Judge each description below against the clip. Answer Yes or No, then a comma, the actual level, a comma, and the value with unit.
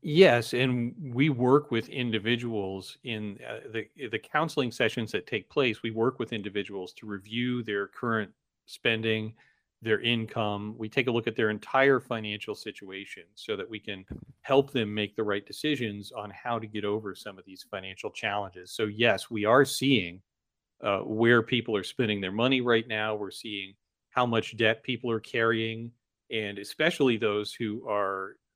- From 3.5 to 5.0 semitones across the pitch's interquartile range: No, narrow, 2.6 semitones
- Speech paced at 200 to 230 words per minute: No, average, 170 wpm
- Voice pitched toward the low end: Yes, low, 110 Hz